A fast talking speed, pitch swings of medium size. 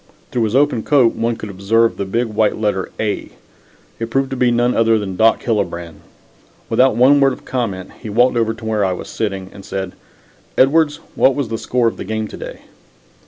Yes: fast, 210 wpm; average, 3.4 semitones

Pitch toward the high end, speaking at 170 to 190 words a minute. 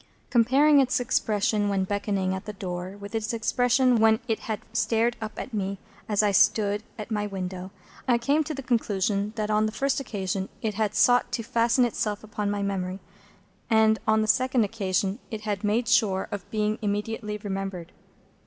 Yes: high, 215 Hz; average, 185 wpm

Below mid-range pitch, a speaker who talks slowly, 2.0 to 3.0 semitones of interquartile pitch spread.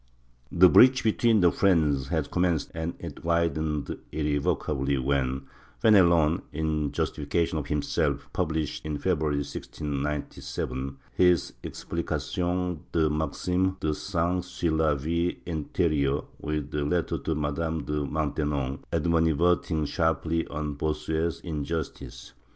Yes: very low, 80 Hz; slow, 115 wpm; narrow, 2.6 semitones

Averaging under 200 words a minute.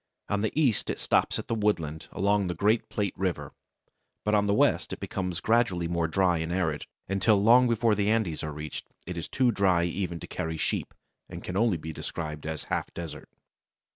No: fast, 205 wpm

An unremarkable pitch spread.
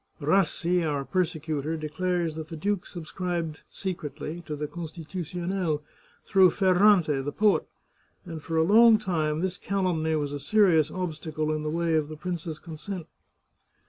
Yes: average, 3.0 semitones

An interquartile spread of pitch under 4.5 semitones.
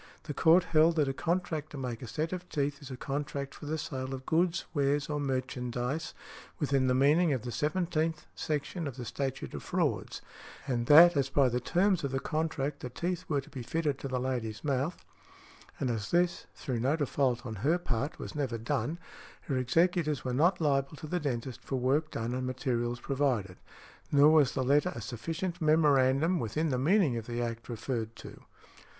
Yes: average, 3.8 semitones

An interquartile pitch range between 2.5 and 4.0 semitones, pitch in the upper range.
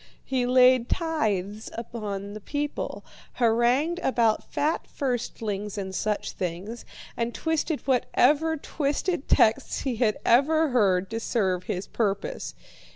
No: average, 5.3 semitones; high, 235 Hz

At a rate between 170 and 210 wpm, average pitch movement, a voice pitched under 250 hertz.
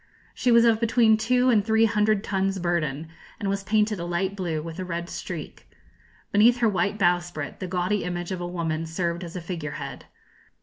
Yes: average, 200 wpm; average, 3.9 semitones; medium, 185 Hz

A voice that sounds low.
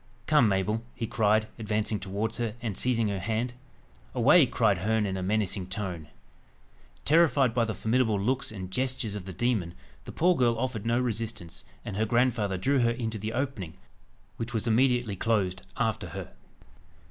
Yes: low, 110 Hz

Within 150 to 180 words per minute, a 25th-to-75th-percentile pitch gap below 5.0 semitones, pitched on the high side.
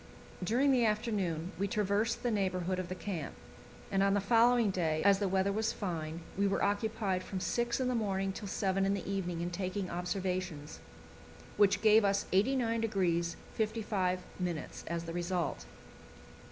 Yes: average, 160 wpm; average, 2.9 semitones; high, 195 Hz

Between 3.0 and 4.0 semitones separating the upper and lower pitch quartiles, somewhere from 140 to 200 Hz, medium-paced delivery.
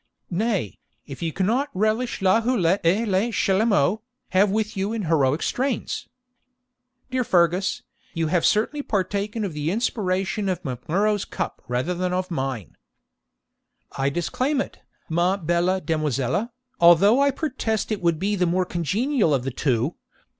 No: average, 4.6 semitones; medium, 185 Hz; average, 150 wpm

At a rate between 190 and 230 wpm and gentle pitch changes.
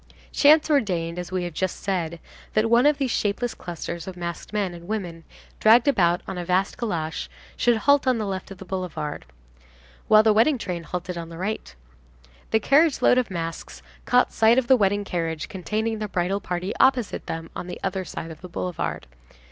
No: average, 195 wpm; average, 4.5 semitones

